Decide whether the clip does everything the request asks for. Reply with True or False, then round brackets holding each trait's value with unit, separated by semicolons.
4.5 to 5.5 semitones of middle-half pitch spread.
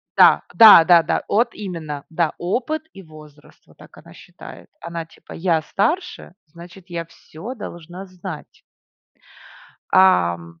False (3.6 semitones)